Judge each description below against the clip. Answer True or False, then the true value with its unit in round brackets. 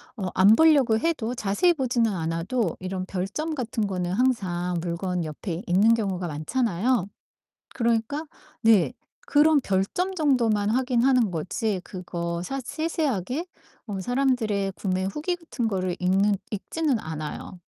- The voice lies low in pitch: False (215 Hz)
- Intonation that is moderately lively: False (5.8 semitones)